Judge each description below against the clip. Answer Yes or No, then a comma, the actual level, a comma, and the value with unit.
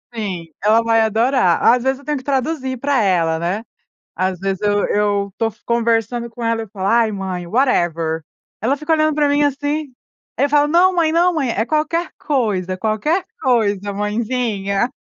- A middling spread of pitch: No, wide, 6.0 semitones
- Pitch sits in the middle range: No, high, 230 Hz